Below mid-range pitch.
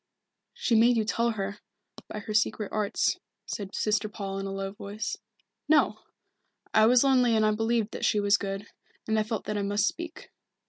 No: high, 215 Hz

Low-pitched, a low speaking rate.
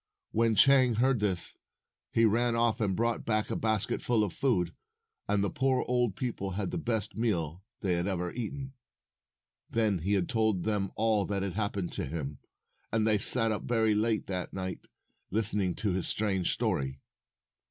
No: low, 105 Hz; average, 175 wpm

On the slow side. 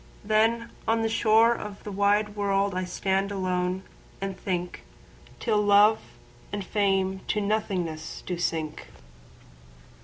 Yes: slow, 115 wpm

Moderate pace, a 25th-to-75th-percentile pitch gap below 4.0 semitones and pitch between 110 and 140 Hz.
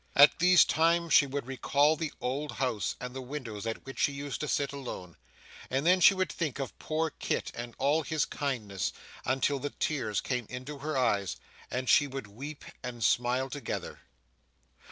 Yes: average, 180 wpm; average, 3.2 semitones; low, 135 Hz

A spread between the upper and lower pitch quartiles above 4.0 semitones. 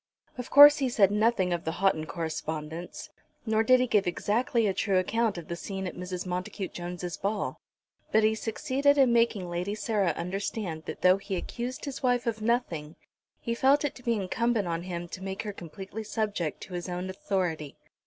Yes: average, 4.7 semitones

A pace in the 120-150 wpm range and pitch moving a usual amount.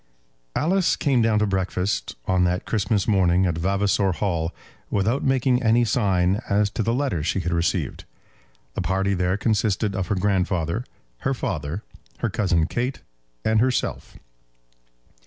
Yes: average, 145 wpm; average, 3.9 semitones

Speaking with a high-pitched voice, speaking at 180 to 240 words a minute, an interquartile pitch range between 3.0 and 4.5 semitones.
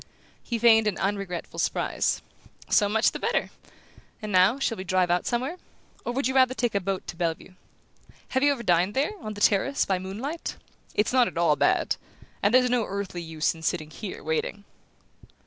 No: high, 205 Hz; average, 190 wpm; average, 5.0 semitones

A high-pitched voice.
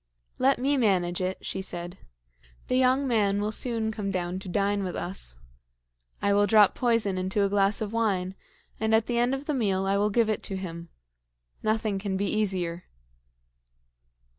Yes: high, 205 Hz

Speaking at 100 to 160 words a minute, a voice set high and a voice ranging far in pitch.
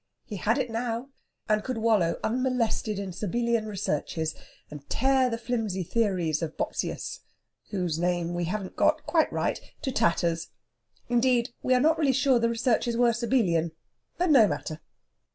Yes: average, 155 wpm; high, 225 Hz; wide, 5.8 semitones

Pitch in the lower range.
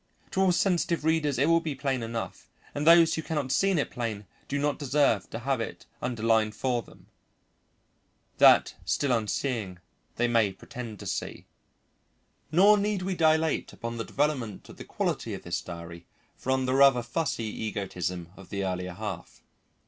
Yes: low, 125 Hz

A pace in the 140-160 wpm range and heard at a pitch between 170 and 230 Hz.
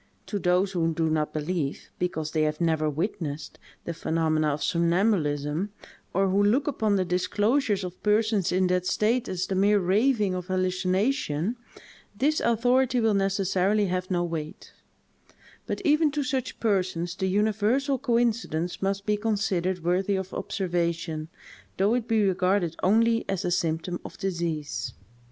Yes: average, 150 wpm; high, 190 Hz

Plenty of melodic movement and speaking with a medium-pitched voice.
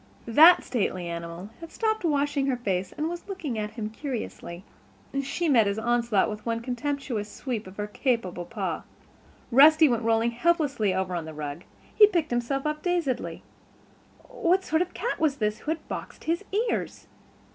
No: wide, 7.0 semitones; high, 245 Hz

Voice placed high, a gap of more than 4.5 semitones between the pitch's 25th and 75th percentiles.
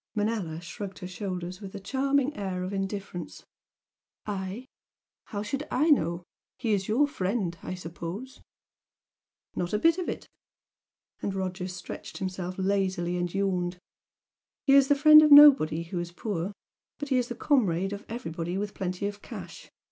Yes: high, 195 Hz; average, 5.0 semitones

